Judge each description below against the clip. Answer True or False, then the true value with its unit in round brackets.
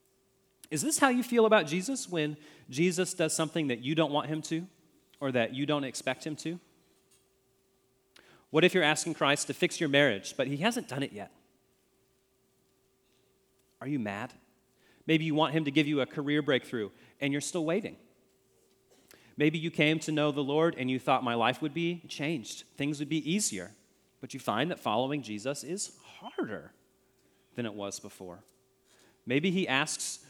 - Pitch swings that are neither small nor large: True (3.4 semitones)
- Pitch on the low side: False (150 Hz)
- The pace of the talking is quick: False (180 wpm)